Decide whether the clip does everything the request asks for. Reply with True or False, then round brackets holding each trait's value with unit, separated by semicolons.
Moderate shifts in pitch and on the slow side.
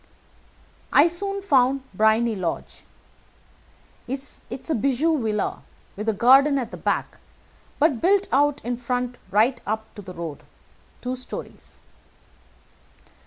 True (4.5 semitones; 130 wpm)